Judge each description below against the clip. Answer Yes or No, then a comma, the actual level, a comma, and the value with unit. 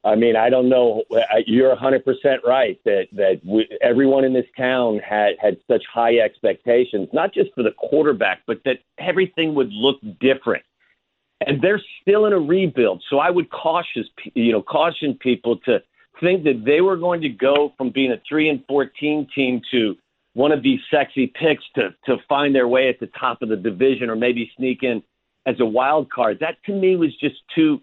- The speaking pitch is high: No, low, 135 Hz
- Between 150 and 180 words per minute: No, average, 195 wpm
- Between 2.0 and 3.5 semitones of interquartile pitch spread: No, average, 4.3 semitones